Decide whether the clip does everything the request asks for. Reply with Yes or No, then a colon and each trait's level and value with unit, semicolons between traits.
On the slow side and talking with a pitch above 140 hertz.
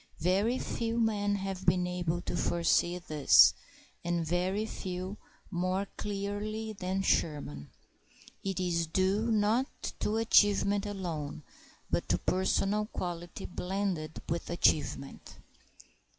Yes: slow, 110 wpm; medium, 185 Hz